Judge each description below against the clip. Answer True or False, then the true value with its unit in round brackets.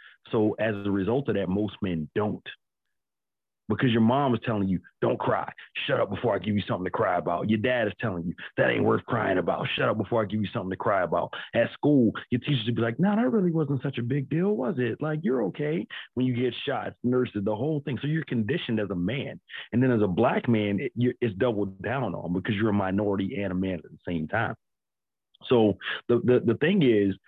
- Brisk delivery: True (240 wpm)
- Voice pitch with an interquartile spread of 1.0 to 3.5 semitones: False (4.2 semitones)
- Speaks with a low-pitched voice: True (115 Hz)